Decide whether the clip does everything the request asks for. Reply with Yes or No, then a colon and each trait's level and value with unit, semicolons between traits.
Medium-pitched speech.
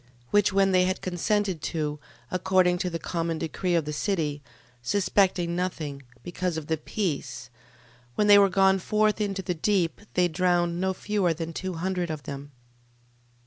Yes: medium, 180 Hz